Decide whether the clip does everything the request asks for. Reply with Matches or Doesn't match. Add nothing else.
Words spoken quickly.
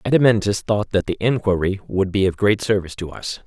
Matches